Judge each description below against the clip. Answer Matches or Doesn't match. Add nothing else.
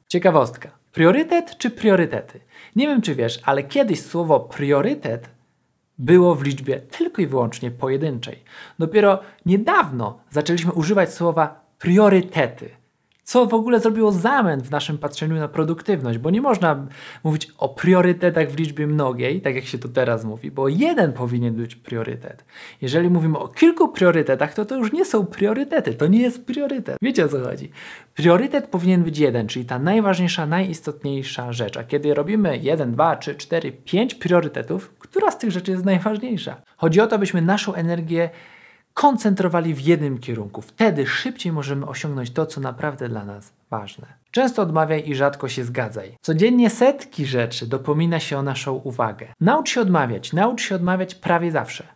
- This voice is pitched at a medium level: Matches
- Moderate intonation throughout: Doesn't match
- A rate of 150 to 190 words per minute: Matches